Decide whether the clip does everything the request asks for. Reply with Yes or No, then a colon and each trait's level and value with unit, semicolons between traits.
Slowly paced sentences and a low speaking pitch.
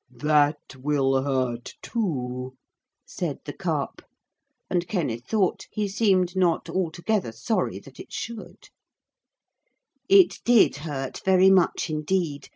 No: slow, 115 wpm; medium, 160 Hz